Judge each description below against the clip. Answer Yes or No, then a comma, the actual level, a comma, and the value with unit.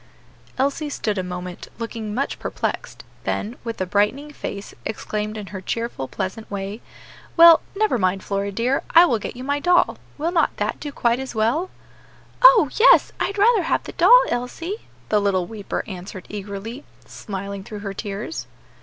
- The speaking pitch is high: Yes, high, 225 Hz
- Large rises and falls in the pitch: Yes, wide, 6.4 semitones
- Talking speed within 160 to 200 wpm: Yes, average, 170 wpm